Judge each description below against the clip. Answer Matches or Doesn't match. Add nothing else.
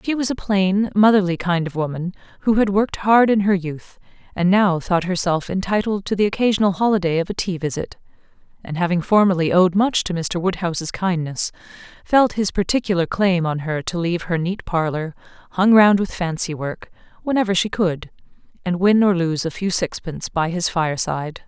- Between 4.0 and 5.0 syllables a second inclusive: Doesn't match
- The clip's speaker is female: Matches